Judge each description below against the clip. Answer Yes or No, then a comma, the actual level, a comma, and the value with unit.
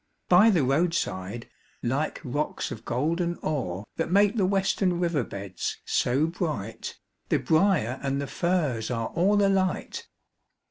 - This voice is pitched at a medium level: Yes, medium, 155 Hz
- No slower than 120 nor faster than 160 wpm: Yes, slow, 135 wpm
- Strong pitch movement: Yes, wide, 6.8 semitones